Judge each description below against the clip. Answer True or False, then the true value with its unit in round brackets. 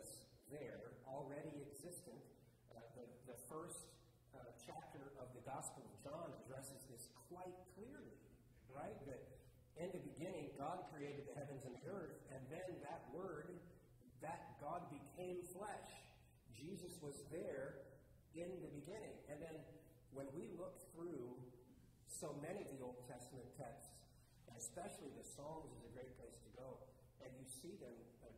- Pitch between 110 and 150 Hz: True (140 Hz)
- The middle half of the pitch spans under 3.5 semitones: False (4.5 semitones)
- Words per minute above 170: False (150 wpm)